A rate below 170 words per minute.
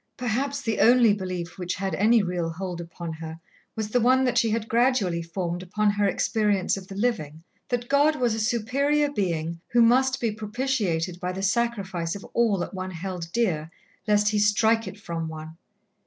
No: average, 185 wpm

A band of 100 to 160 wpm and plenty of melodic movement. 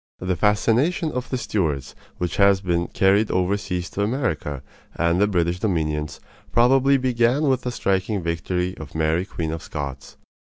Yes: average, 155 wpm; wide, 5.7 semitones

